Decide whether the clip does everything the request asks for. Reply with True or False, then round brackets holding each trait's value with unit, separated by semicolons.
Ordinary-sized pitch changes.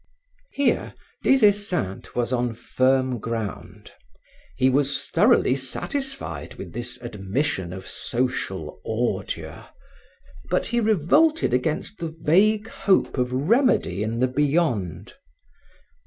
False (8.2 semitones)